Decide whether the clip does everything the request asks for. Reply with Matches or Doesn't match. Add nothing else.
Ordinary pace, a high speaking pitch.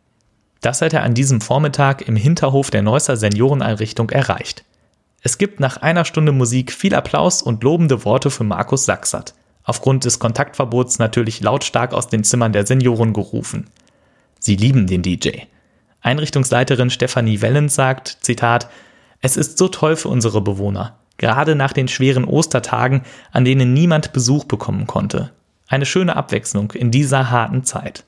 Doesn't match